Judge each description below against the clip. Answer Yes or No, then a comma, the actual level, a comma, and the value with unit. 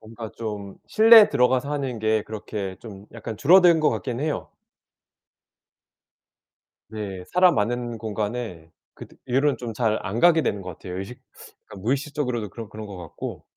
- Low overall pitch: Yes, low, 115 Hz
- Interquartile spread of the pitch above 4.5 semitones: Yes, average, 4.9 semitones